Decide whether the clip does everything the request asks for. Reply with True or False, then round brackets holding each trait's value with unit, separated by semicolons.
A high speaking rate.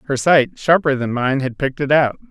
True (235 wpm)